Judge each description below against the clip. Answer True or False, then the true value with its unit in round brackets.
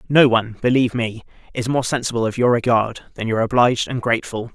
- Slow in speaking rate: False (200 wpm)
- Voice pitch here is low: True (120 Hz)